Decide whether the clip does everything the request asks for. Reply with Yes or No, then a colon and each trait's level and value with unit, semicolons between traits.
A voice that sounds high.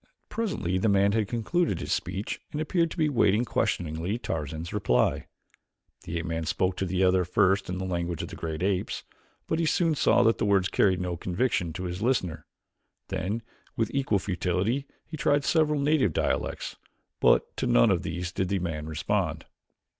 No: very low, 95 Hz